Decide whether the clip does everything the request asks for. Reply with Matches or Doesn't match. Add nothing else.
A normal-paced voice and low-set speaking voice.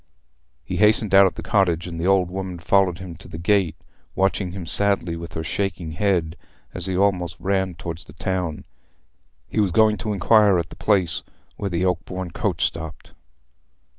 Matches